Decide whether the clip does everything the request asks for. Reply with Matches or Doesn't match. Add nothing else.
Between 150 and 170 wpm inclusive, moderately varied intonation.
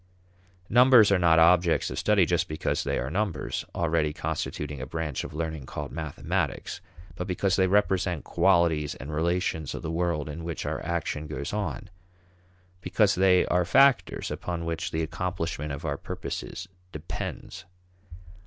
Matches